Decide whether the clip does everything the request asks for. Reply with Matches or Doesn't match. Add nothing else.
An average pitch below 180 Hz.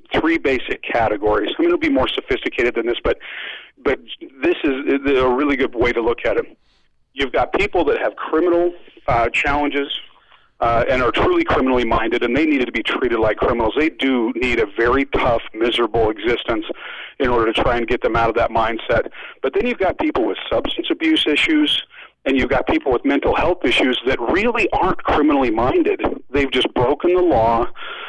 Doesn't match